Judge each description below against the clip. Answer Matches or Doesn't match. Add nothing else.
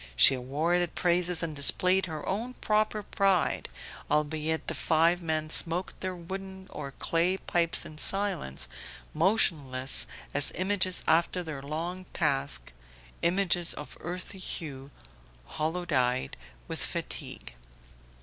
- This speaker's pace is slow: Matches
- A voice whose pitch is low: Doesn't match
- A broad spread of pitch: Doesn't match